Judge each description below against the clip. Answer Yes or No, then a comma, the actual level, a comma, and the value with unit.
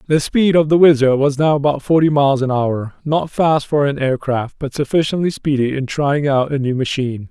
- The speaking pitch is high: No, medium, 140 Hz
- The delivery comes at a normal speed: No, fast, 220 wpm